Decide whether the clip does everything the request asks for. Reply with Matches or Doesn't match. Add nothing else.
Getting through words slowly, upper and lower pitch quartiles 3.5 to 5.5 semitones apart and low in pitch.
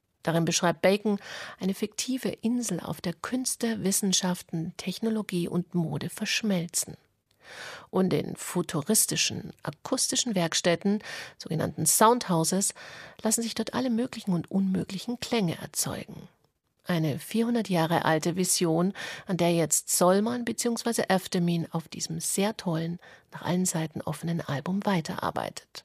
Doesn't match